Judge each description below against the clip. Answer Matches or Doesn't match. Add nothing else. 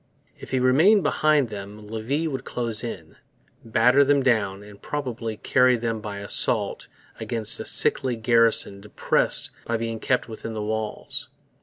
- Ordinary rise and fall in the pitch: Matches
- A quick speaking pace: Doesn't match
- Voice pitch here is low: Matches